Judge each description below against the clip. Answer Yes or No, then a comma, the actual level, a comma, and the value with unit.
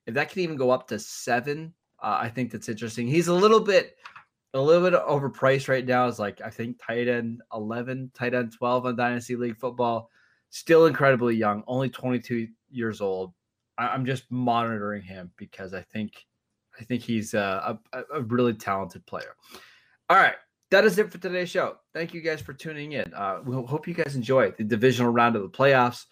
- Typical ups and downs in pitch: Yes, average, 3.1 semitones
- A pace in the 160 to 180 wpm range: No, average, 200 wpm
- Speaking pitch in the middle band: No, low, 125 Hz